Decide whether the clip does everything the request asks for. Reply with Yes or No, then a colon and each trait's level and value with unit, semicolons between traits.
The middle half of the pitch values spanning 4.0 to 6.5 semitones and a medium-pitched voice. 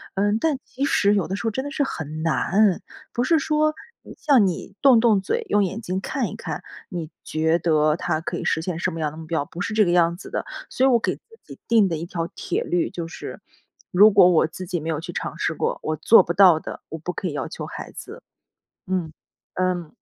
Yes: average, 4.9 semitones; medium, 180 Hz